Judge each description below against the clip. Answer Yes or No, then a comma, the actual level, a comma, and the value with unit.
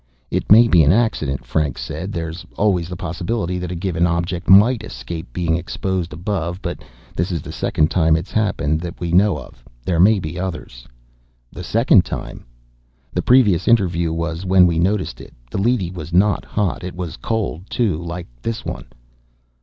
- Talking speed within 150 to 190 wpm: Yes, average, 180 wpm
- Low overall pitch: Yes, very low, 90 Hz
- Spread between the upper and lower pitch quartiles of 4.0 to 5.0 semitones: No, average, 2.9 semitones